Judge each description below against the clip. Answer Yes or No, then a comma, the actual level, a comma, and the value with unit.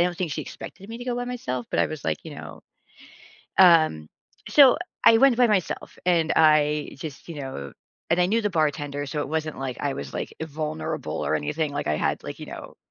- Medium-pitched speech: Yes, medium, 155 Hz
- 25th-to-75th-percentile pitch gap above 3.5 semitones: Yes, average, 4.6 semitones